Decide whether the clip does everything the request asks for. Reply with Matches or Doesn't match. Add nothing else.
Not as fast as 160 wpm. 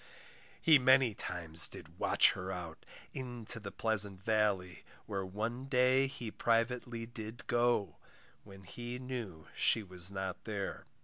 Matches